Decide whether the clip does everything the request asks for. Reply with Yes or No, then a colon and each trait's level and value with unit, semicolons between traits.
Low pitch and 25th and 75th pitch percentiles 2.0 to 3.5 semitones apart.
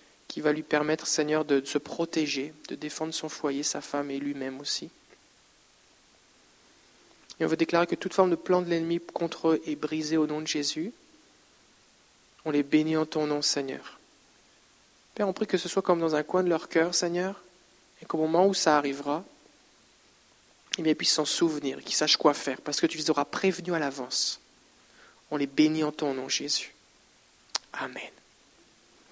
No: medium, 155 Hz; narrow, 2.4 semitones